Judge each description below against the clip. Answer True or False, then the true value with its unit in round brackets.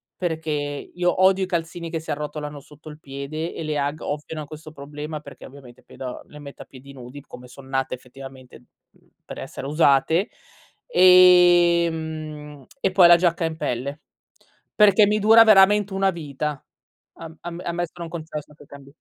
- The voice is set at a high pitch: False (155 Hz)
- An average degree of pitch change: True (3.5 semitones)